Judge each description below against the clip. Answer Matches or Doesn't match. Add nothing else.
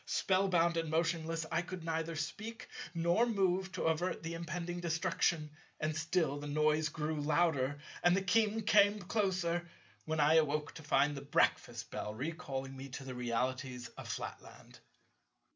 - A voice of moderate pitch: Matches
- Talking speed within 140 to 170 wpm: Matches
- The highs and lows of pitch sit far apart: Doesn't match